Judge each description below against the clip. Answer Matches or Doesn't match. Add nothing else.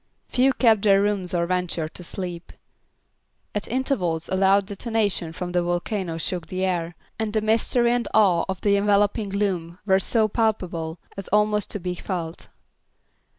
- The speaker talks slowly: Doesn't match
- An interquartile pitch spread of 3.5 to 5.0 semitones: Doesn't match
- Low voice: Doesn't match